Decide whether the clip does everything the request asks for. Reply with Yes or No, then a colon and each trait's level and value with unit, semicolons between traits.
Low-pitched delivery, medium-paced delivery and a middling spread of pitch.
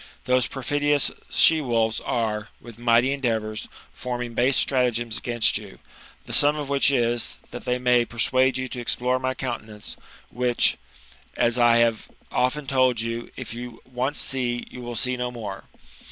No: low, 125 Hz; average, 160 wpm; narrow, 1.8 semitones